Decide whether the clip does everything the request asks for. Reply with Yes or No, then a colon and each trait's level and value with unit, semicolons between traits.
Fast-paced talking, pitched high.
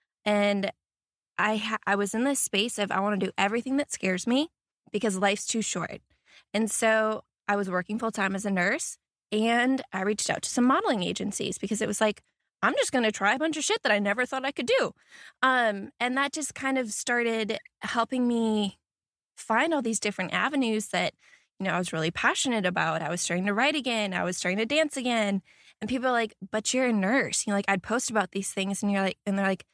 Yes: fast, 230 wpm; high, 220 Hz